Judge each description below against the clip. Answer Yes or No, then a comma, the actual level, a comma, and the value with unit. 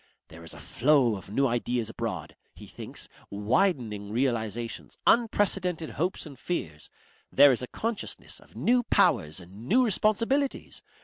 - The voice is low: Yes, low, 125 Hz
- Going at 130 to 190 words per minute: Yes, average, 140 wpm